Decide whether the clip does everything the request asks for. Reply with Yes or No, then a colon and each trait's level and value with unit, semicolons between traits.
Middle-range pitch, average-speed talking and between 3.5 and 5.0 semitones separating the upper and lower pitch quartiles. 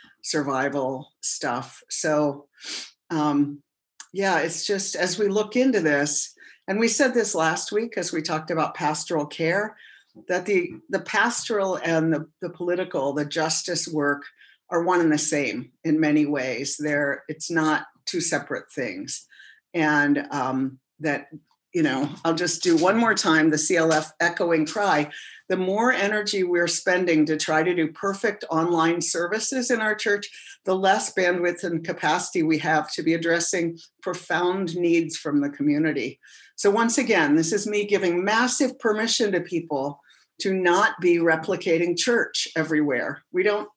Yes: medium, 170 Hz; average, 155 wpm; average, 4.5 semitones